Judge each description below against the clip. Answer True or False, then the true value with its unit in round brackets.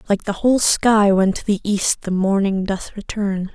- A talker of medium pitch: False (200 Hz)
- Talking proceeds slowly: False (205 wpm)